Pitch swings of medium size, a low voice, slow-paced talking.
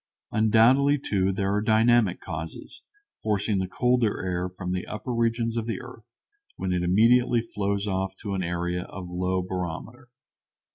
No: average, 3.9 semitones; low, 100 Hz; average, 155 wpm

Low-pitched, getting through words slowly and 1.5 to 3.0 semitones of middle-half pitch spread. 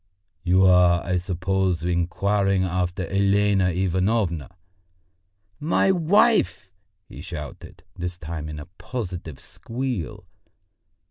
Yes: very low, 90 Hz; slow, 95 wpm; narrow, 2.4 semitones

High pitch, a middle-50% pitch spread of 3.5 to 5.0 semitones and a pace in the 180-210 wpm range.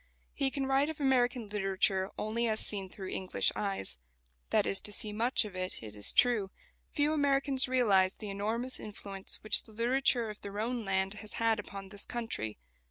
Yes: high, 215 Hz; average, 4.1 semitones; average, 185 wpm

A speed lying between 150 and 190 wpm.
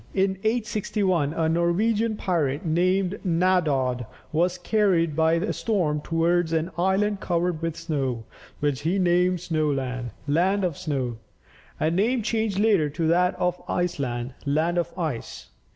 No: slow, 135 wpm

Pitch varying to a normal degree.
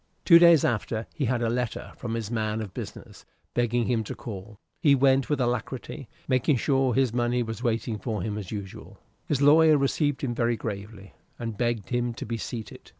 Yes: average, 3.1 semitones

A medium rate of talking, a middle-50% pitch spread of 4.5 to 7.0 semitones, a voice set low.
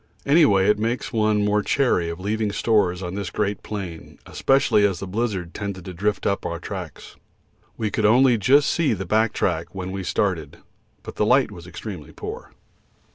No: average, 185 wpm; average, 3.1 semitones; low, 105 Hz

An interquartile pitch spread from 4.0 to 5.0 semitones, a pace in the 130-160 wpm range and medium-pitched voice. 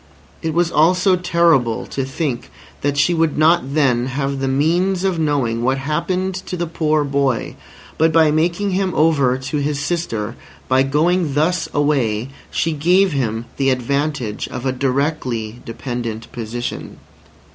Yes: average, 4.3 semitones; average, 150 wpm; medium, 145 Hz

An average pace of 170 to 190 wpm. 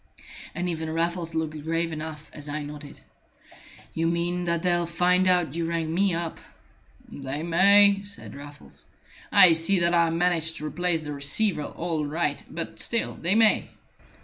No: average, 160 wpm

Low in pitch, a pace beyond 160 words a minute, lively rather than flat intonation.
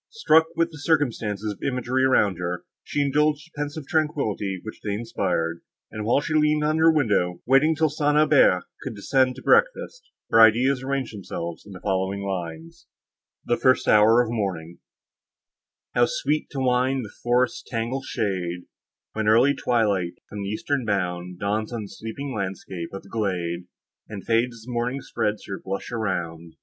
Yes: low, 115 Hz; average, 170 wpm; wide, 5.9 semitones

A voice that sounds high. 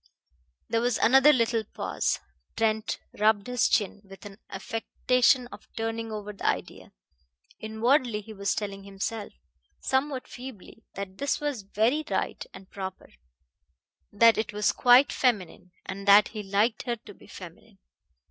Yes: high, 220 Hz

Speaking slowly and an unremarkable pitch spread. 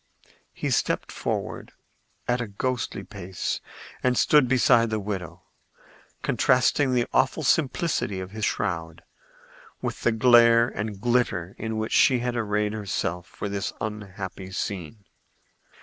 Yes: slow, 130 wpm; average, 3.8 semitones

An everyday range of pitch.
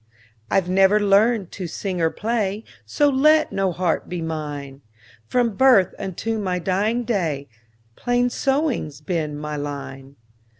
No: wide, 7.2 semitones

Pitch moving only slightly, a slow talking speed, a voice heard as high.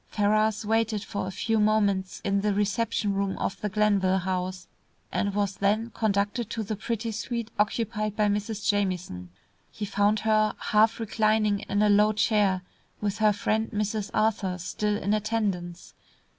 No: narrow, 1.5 semitones; average, 160 wpm; high, 210 Hz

